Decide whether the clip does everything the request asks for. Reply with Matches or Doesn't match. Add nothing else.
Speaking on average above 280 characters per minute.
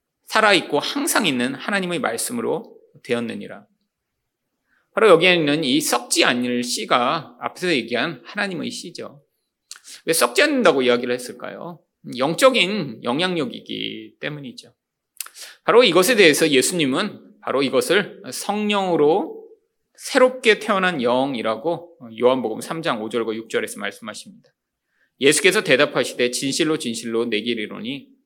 Matches